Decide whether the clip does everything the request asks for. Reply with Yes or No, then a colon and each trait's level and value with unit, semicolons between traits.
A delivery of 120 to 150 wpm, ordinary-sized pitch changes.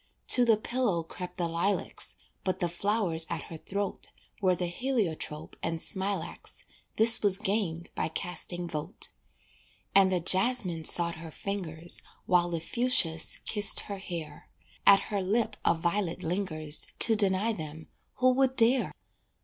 Yes: average, 145 wpm; average, 4.0 semitones